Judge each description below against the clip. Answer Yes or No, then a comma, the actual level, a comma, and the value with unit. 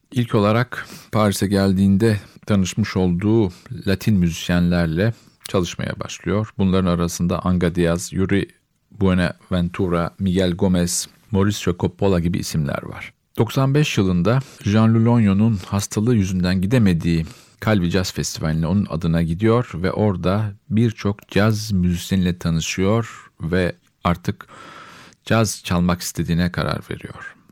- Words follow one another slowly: No, average, 105 wpm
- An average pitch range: Yes, average, 3.5 semitones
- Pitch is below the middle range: Yes, very low, 95 Hz